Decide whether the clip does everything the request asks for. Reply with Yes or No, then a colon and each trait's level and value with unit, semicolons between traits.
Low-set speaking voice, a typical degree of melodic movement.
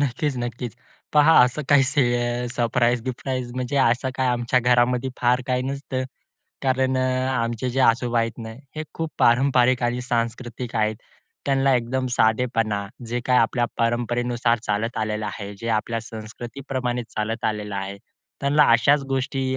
No: low, 120 Hz; narrow, 2.0 semitones